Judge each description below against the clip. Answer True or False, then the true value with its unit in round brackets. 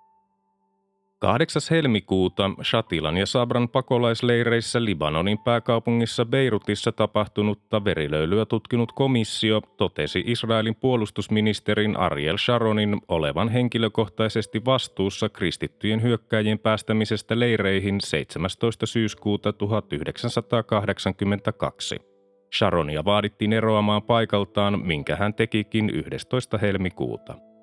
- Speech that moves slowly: True (80 wpm)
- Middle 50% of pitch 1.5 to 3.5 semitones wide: True (2.8 semitones)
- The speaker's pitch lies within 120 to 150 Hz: False (110 Hz)